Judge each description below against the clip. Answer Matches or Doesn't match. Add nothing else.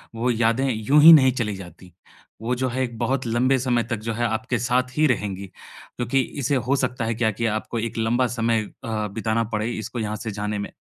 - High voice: Doesn't match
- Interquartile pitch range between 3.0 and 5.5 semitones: Doesn't match